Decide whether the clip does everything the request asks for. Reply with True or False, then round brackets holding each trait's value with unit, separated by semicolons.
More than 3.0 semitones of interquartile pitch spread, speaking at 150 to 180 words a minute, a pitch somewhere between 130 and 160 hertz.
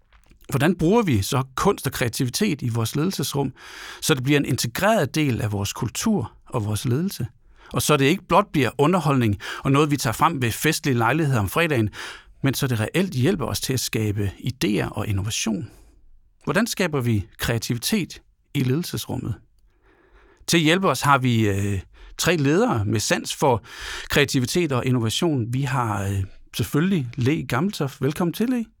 True (5.6 semitones; 170 wpm; 135 Hz)